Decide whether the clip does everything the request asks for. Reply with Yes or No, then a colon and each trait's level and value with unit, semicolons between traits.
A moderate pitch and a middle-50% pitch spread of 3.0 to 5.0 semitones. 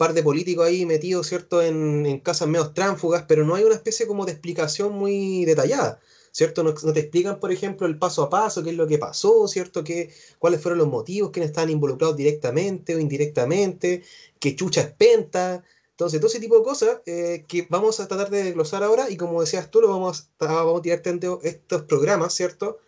Yes: medium, 175 Hz; average, 3.3 semitones